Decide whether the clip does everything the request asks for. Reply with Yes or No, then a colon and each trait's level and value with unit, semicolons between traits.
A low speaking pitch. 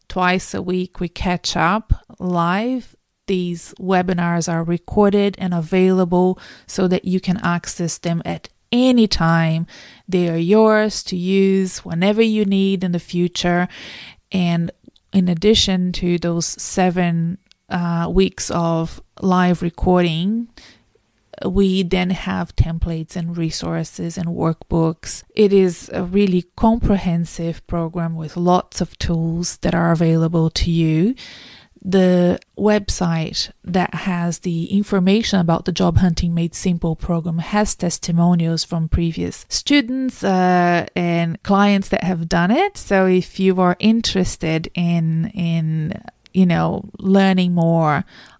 No: medium, 180 Hz